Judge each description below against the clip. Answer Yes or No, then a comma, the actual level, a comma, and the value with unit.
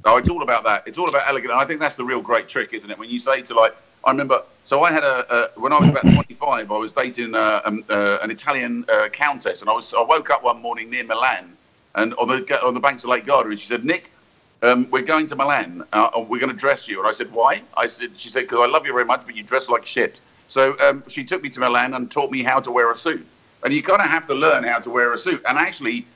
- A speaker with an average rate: No, fast, 295 wpm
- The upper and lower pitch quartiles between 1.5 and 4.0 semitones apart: No, wide, 5.5 semitones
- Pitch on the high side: No, low, 135 Hz